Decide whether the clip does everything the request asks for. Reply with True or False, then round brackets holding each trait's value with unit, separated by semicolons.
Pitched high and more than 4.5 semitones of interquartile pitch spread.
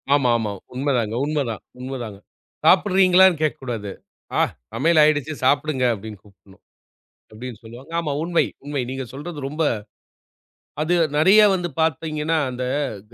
False (140 Hz; 5.1 semitones)